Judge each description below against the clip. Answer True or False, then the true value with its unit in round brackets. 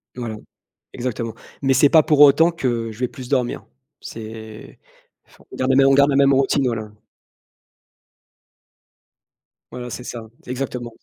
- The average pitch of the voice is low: True (125 Hz)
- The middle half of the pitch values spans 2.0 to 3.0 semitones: True (2.7 semitones)